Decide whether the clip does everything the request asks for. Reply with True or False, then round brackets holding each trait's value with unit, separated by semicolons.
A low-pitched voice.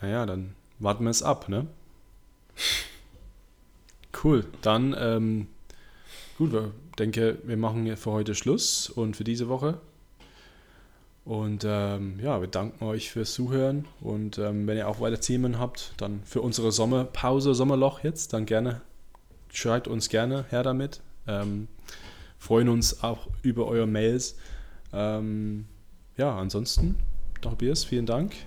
True (110 Hz)